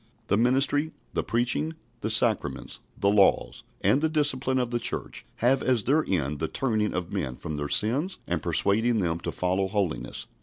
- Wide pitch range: Yes, wide, 6.5 semitones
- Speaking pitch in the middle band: No, low, 110 Hz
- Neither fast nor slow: Yes, average, 180 wpm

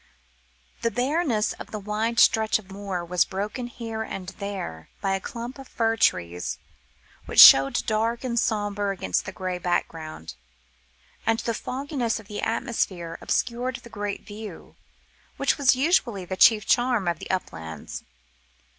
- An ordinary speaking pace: Yes, average, 150 wpm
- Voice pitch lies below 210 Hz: No, high, 215 Hz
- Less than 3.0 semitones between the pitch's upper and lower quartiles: No, average, 4.0 semitones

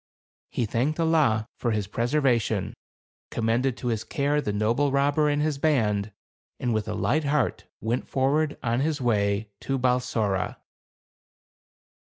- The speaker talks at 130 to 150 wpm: Yes, average, 140 wpm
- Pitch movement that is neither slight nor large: Yes, average, 4.8 semitones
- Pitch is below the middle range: Yes, low, 125 Hz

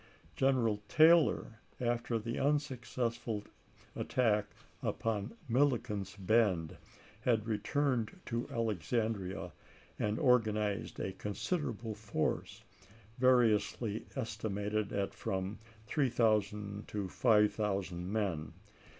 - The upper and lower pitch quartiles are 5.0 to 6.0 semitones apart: No, average, 3.1 semitones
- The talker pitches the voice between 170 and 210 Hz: No, low, 110 Hz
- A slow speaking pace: Yes, slow, 80 wpm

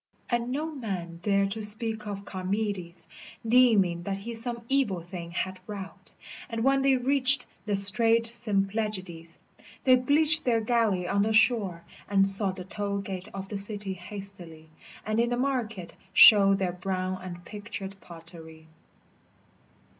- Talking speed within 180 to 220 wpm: No, average, 145 wpm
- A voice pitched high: Yes, high, 200 Hz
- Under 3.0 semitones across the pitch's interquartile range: No, average, 3.6 semitones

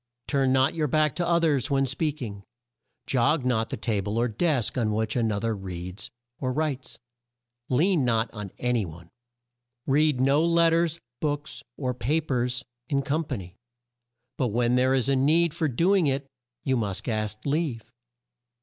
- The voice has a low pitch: Yes, low, 130 Hz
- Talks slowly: No, average, 185 wpm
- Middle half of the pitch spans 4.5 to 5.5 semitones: Yes, average, 5.0 semitones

